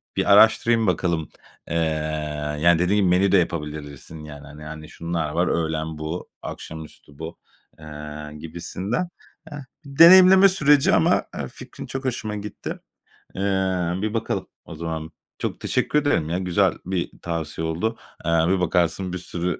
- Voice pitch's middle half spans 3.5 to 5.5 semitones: Yes, average, 5.0 semitones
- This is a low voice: Yes, very low, 85 Hz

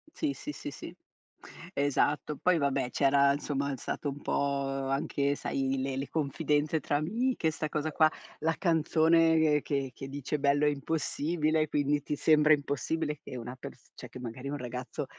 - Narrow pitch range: Yes, narrow, 2.2 semitones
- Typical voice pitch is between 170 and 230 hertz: No, medium, 145 Hz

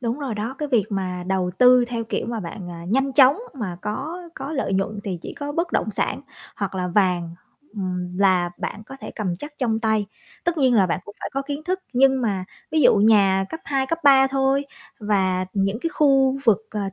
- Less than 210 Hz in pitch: No, high, 220 Hz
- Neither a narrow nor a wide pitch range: No, wide, 6.0 semitones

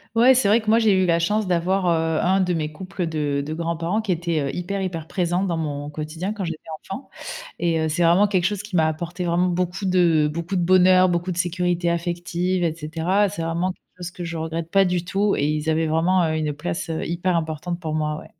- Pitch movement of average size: No, narrow, 2.3 semitones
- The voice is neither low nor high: Yes, medium, 175 Hz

